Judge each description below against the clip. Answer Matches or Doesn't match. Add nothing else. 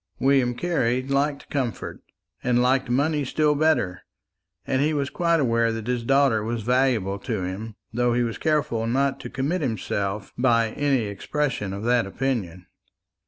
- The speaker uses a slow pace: Doesn't match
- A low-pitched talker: Matches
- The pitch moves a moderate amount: Matches